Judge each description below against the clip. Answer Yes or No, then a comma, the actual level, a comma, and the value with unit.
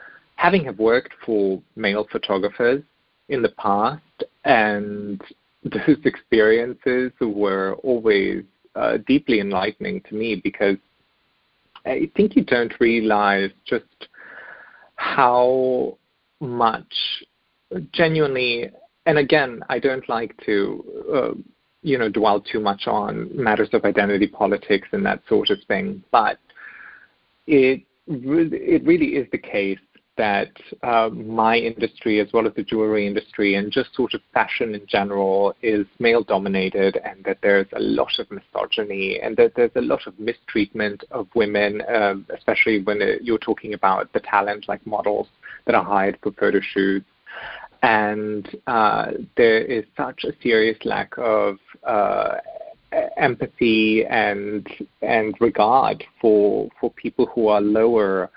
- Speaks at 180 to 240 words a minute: No, slow, 135 wpm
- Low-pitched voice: Yes, low, 110 Hz